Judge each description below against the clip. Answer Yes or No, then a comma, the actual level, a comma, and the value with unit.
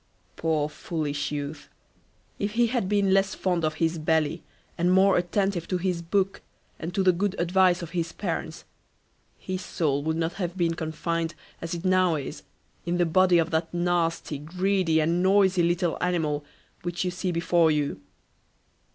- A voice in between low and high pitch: Yes, medium, 175 Hz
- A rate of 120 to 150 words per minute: No, average, 170 wpm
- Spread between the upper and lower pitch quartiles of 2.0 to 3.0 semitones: Yes, narrow, 2.5 semitones